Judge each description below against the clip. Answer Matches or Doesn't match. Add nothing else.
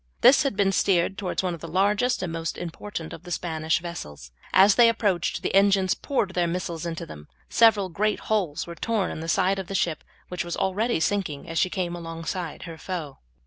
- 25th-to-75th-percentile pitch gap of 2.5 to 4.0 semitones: Matches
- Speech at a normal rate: Doesn't match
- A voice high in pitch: Doesn't match